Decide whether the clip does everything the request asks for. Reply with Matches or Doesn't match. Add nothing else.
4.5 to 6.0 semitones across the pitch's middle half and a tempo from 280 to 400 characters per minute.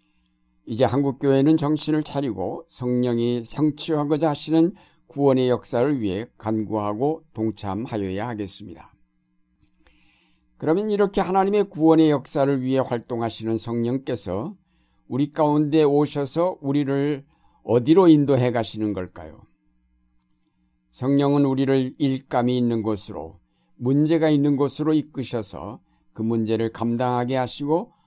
Matches